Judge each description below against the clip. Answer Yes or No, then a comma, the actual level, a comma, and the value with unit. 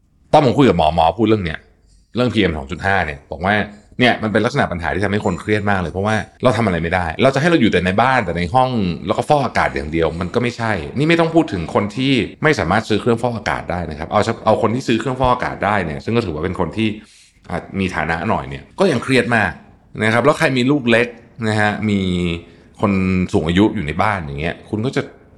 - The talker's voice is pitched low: Yes, low, 105 Hz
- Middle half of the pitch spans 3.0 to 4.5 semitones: No, average, 5.1 semitones